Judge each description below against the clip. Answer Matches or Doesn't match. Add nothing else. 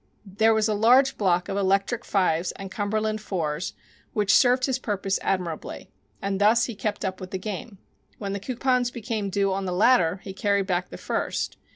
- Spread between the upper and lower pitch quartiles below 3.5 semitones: Matches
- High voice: Matches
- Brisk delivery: Doesn't match